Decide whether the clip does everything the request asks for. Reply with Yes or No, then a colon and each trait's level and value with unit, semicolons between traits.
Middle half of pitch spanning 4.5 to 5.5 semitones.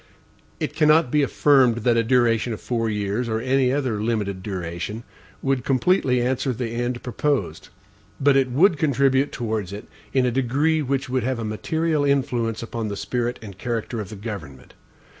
No: average, 3.5 semitones